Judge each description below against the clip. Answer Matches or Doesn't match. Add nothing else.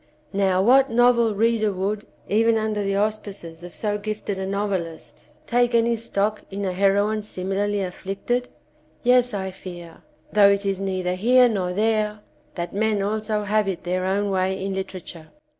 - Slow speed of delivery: Doesn't match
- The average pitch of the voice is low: Doesn't match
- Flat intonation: Matches